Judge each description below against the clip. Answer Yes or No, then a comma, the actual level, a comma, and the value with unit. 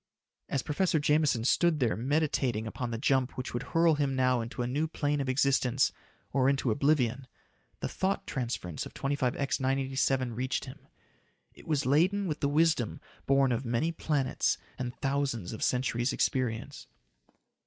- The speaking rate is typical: Yes, average, 155 wpm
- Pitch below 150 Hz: Yes, low, 135 Hz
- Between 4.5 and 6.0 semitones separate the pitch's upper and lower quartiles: No, average, 2.8 semitones